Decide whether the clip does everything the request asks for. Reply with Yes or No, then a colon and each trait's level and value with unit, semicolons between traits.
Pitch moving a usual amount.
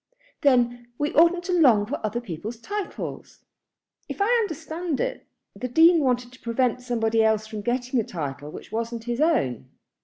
No: wide, 6.0 semitones